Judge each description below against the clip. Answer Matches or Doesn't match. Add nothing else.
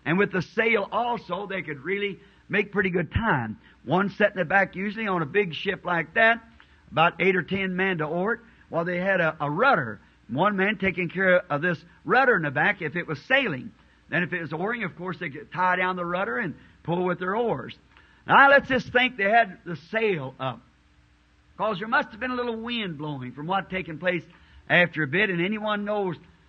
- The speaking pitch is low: Doesn't match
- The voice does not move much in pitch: Doesn't match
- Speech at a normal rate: Doesn't match